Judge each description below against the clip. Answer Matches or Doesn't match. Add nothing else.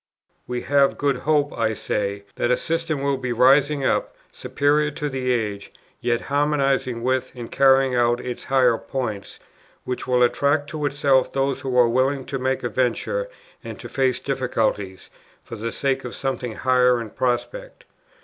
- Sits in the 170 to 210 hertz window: Doesn't match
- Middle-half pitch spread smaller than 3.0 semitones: Matches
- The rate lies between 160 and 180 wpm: Matches